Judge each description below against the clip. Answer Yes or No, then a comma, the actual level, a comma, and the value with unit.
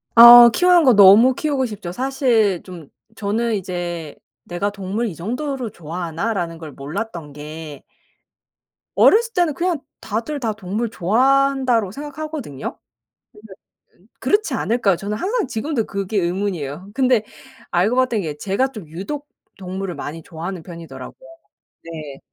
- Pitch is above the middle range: Yes, high, 205 Hz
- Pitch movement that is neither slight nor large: No, wide, 6.8 semitones